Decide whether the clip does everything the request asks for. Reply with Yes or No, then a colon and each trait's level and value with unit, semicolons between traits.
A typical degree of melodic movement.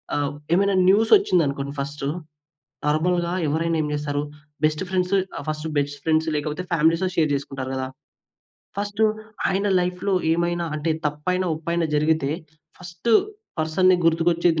Yes: average, 3.3 semitones